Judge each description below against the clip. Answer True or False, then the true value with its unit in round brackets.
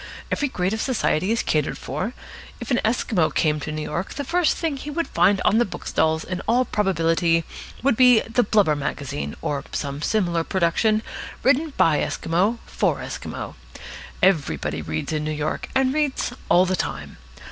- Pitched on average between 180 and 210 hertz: True (185 Hz)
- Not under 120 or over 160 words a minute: False (170 wpm)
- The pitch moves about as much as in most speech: False (7.7 semitones)